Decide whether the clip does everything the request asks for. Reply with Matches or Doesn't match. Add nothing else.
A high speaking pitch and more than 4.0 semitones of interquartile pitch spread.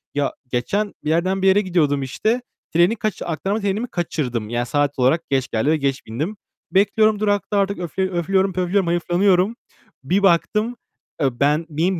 Doesn't match